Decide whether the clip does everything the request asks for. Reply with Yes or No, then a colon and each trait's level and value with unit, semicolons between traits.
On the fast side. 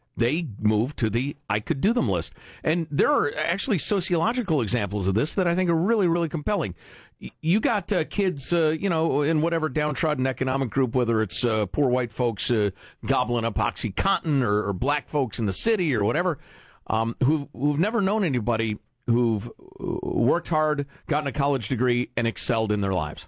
No: average, 190 wpm